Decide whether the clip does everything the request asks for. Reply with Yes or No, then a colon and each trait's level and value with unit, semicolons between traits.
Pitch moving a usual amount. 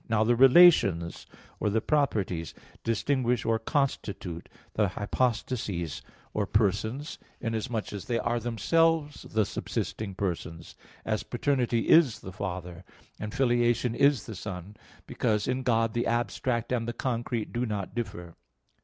Yes: average, 3.5 semitones